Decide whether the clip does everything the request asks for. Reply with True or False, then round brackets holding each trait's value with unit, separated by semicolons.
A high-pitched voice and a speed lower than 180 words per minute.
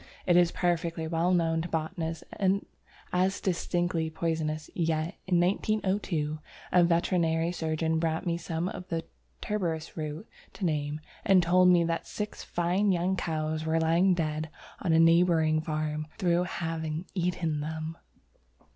False (165 Hz; 140 wpm)